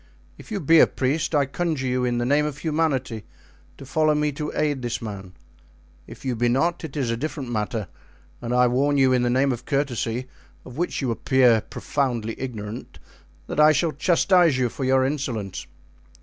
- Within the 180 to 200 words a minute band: Yes, average, 190 wpm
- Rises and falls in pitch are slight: No, average, 3.7 semitones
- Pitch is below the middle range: Yes, low, 130 Hz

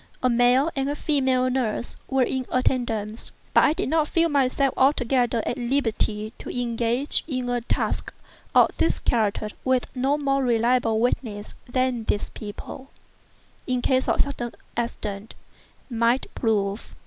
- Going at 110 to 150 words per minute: Yes, average, 145 wpm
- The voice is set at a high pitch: Yes, very high, 250 Hz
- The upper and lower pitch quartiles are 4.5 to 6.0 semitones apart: No, average, 2.7 semitones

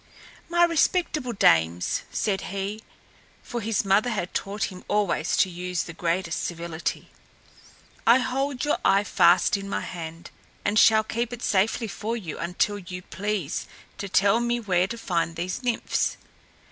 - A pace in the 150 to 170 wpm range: Yes, average, 155 wpm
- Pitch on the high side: Yes, high, 200 Hz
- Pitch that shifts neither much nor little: Yes, average, 4.5 semitones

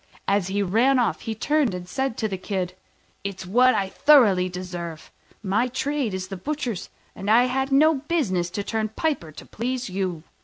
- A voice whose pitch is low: No, high, 210 Hz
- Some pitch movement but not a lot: No, wide, 5.7 semitones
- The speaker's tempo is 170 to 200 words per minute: Yes, average, 185 wpm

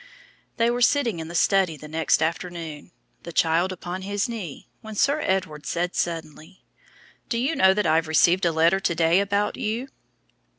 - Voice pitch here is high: No, medium, 180 Hz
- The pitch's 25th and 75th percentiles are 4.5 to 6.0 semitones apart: No, average, 3.9 semitones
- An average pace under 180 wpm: No, average, 185 wpm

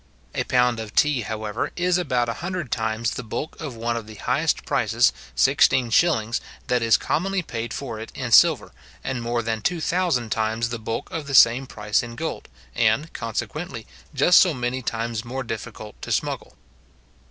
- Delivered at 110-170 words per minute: No, average, 180 wpm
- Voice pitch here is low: Yes, low, 120 Hz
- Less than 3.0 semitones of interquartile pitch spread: No, average, 3.9 semitones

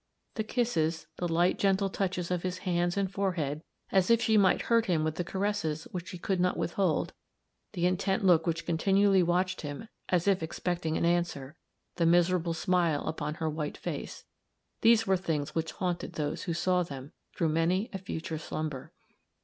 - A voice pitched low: No, medium, 175 Hz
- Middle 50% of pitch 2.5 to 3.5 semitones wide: Yes, average, 2.9 semitones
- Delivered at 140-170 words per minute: No, average, 180 wpm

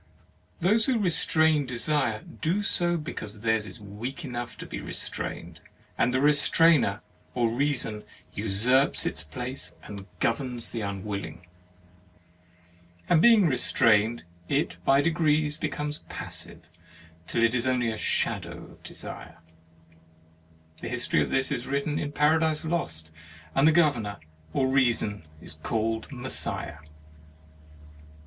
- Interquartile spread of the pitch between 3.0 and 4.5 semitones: No, wide, 5.6 semitones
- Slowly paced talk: Yes, slow, 125 wpm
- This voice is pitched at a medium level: No, low, 130 Hz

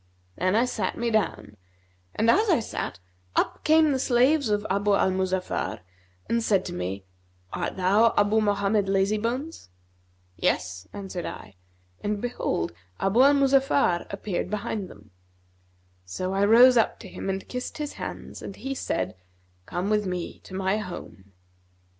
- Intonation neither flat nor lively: Yes, average, 4.3 semitones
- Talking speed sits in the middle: Yes, average, 155 wpm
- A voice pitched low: No, high, 205 Hz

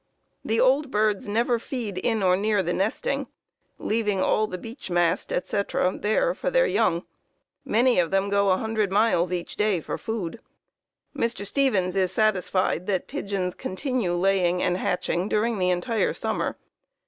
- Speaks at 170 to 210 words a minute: No, average, 155 wpm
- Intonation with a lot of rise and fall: No, average, 3.7 semitones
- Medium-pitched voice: No, high, 200 Hz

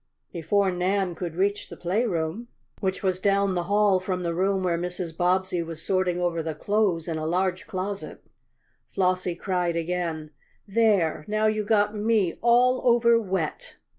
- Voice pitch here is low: No, medium, 185 Hz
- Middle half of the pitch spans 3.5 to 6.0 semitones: No, average, 2.9 semitones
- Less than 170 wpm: Yes, average, 160 wpm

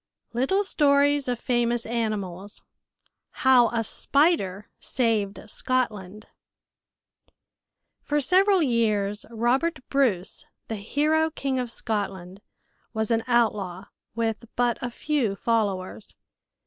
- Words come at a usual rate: No, slow, 100 wpm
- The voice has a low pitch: No, high, 235 Hz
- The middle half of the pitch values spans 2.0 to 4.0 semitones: No, average, 4.7 semitones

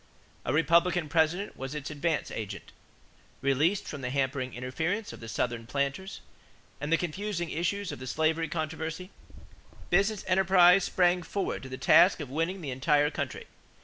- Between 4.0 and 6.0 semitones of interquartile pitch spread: Yes, average, 4.5 semitones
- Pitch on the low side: No, medium, 160 Hz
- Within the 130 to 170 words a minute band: Yes, average, 155 wpm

